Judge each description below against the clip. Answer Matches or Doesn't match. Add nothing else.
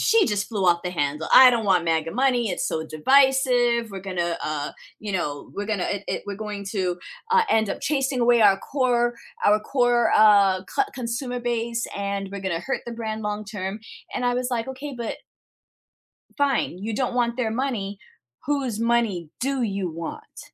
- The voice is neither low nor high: Doesn't match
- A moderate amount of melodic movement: Matches